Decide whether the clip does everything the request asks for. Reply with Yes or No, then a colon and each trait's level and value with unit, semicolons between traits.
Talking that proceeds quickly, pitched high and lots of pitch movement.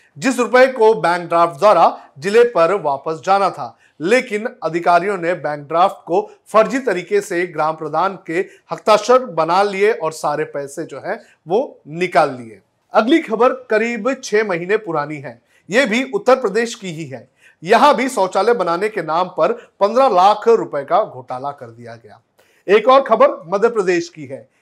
No: average, 170 wpm; high, 200 Hz; wide, 7.3 semitones